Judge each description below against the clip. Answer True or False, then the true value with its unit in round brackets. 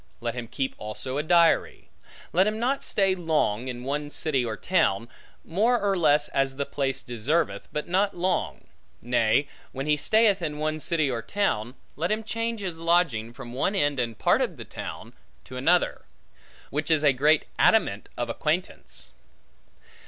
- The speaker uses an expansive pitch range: True (5.8 semitones)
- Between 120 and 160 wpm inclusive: False (170 wpm)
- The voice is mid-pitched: True (150 Hz)